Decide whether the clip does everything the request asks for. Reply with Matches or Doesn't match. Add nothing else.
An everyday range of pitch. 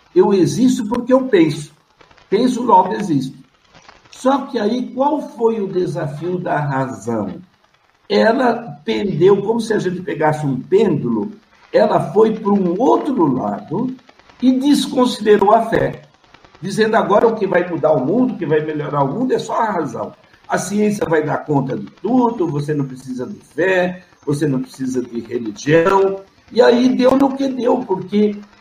Doesn't match